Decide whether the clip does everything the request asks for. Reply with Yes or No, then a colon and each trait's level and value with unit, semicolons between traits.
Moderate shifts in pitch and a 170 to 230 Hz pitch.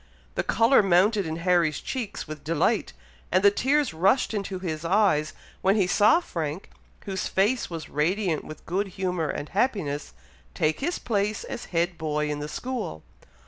Yes: average, 4.7 semitones; medium, 185 Hz